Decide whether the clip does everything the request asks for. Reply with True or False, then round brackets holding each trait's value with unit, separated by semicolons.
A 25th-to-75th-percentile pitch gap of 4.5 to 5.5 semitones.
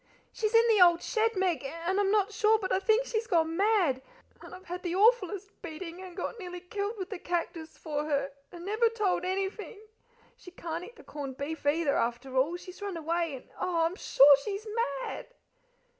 False (3.9 semitones)